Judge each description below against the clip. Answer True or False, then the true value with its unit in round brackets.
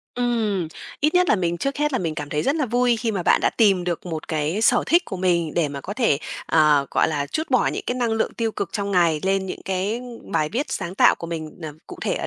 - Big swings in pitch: True (6.6 semitones)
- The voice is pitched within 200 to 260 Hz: False (190 Hz)